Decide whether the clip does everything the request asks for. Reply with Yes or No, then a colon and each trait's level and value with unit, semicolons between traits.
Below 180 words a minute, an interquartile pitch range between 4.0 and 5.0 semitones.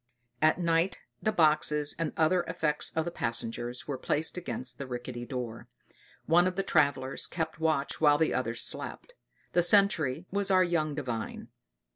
Yes: average, 160 wpm; average, 4.6 semitones